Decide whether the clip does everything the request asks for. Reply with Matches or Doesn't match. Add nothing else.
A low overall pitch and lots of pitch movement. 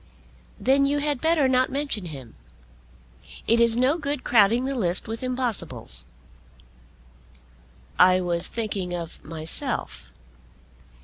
Doesn't match